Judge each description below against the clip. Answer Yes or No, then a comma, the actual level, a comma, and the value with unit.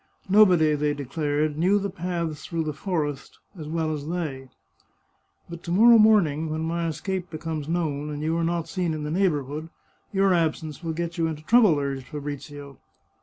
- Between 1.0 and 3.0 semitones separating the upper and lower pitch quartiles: Yes, average, 2.7 semitones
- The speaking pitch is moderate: Yes, medium, 160 Hz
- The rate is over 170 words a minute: Yes, average, 180 wpm